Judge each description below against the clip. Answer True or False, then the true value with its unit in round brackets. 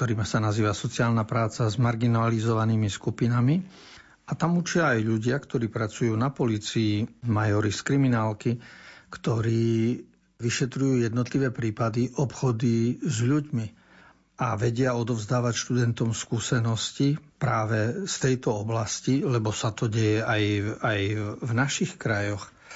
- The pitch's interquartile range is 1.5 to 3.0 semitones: True (2.6 semitones)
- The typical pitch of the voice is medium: False (120 Hz)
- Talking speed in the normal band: True (120 wpm)